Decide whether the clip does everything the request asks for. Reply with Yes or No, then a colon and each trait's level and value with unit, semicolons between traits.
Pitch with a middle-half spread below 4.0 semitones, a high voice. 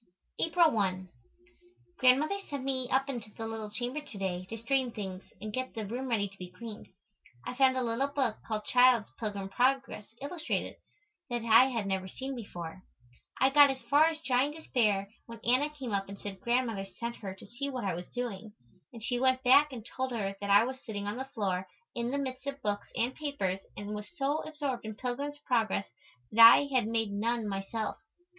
No: average, 4.3 semitones; high, 235 Hz